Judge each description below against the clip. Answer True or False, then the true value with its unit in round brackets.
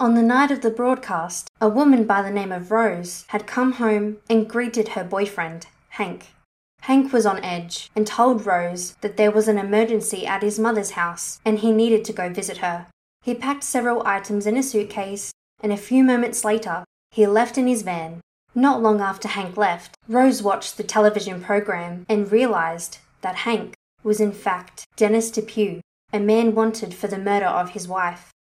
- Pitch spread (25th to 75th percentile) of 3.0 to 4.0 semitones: True (3.5 semitones)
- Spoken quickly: False (185 wpm)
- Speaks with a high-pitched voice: True (210 Hz)